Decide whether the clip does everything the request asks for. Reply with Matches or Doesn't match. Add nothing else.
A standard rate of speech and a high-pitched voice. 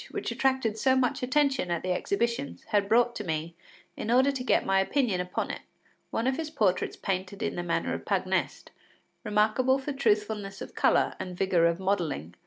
Matches